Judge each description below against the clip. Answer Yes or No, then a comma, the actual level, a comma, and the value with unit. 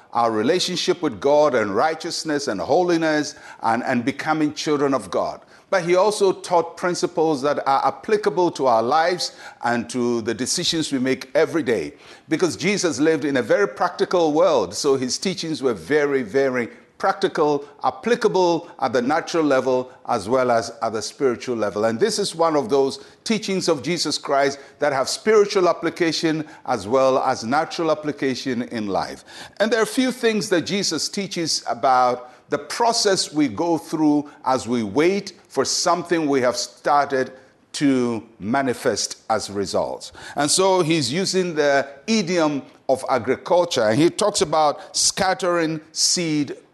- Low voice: No, medium, 155 Hz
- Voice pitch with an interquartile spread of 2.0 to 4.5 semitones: No, average, 5.0 semitones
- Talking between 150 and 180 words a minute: Yes, average, 155 wpm